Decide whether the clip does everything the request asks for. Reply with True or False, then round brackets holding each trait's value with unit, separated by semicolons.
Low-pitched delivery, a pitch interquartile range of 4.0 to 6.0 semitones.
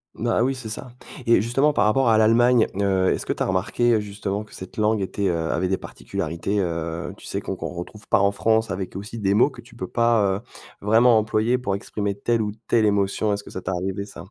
False (105 Hz; 2.9 semitones)